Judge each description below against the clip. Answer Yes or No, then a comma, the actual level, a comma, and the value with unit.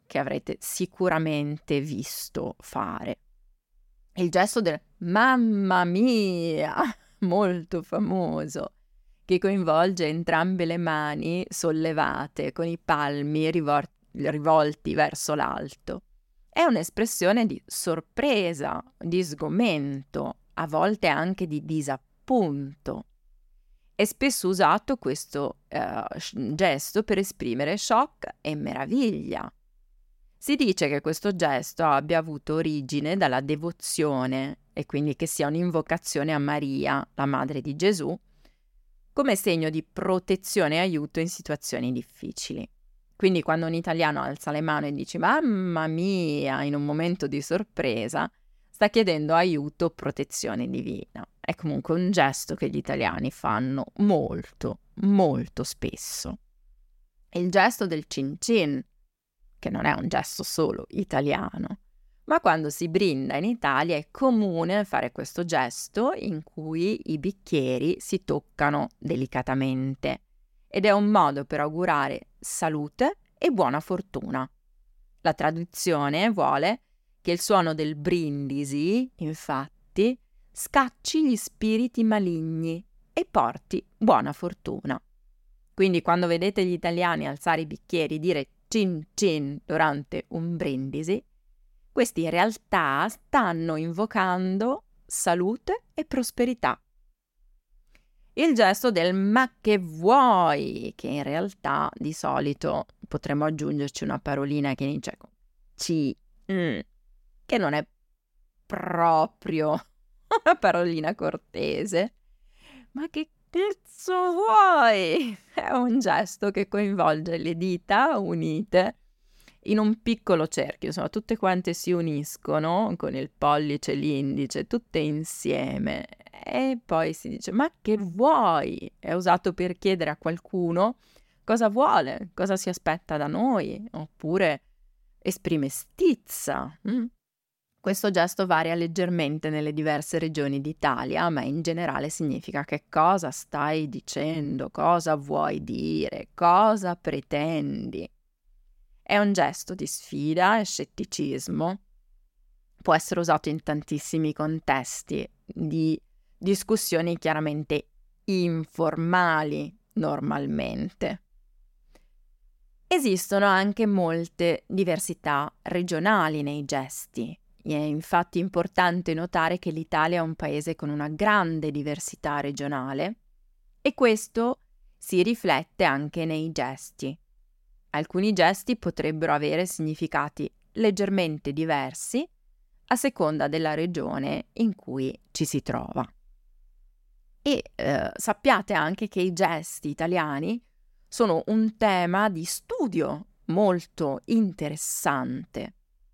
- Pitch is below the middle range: No, medium, 170 Hz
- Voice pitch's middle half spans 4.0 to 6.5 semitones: Yes, average, 4.9 semitones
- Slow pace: Yes, slow, 110 wpm